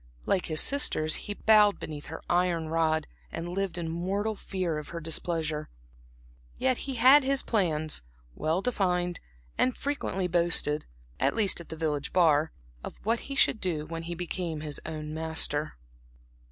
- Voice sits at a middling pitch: Yes, medium, 170 Hz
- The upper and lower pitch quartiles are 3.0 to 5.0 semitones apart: Yes, average, 3.9 semitones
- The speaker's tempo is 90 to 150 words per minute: No, average, 160 wpm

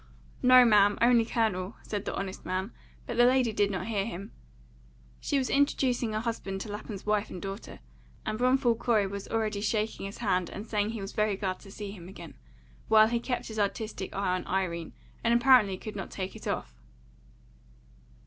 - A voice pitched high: Yes, high, 210 Hz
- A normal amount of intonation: Yes, average, 3.0 semitones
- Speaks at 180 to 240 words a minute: Yes, average, 190 wpm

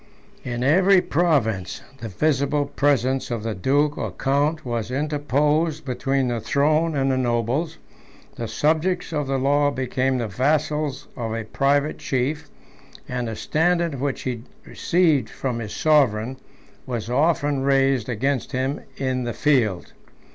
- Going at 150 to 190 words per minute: No, average, 140 wpm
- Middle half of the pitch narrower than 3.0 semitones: No, average, 3.5 semitones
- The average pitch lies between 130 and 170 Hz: Yes, low, 135 Hz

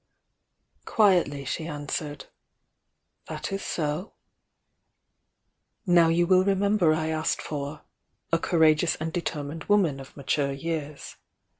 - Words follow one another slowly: Yes, slow, 115 wpm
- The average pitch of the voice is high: No, medium, 160 Hz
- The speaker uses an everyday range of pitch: Yes, average, 3.2 semitones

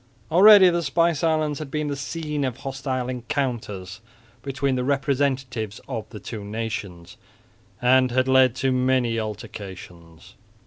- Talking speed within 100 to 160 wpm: Yes, slow, 135 wpm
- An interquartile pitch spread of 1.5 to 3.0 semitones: No, average, 4.0 semitones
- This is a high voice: No, low, 130 Hz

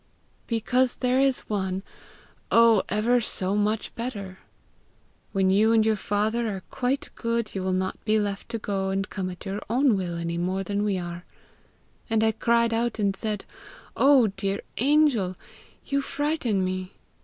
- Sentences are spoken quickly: No, average, 165 wpm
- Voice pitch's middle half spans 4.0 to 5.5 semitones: No, average, 3.4 semitones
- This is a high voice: Yes, high, 210 Hz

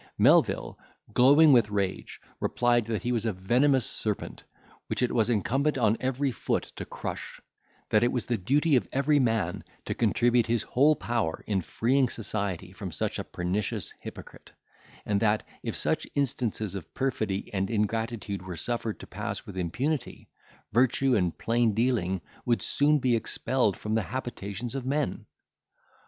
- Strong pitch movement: No, average, 4.1 semitones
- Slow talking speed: No, average, 160 wpm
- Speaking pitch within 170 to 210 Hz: No, low, 115 Hz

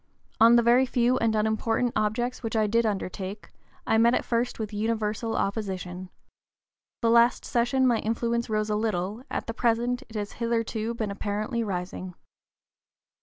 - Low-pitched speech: No, high, 225 Hz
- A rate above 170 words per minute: No, average, 160 wpm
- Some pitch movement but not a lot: No, narrow, 2.0 semitones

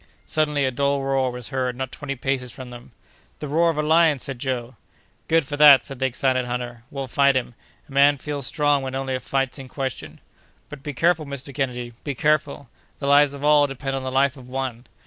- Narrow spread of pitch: Yes, narrow, 2.0 semitones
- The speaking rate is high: Yes, fast, 220 wpm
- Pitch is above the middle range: No, low, 135 Hz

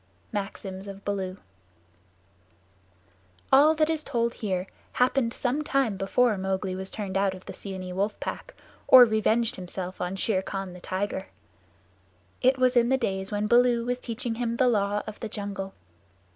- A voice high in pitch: Yes, high, 210 Hz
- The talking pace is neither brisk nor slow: Yes, average, 160 wpm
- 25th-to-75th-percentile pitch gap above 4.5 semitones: No, average, 4.2 semitones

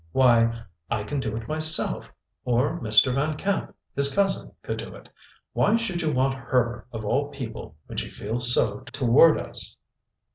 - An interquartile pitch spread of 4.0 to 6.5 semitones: Yes, average, 4.7 semitones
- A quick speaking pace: No, average, 170 wpm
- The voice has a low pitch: Yes, low, 130 Hz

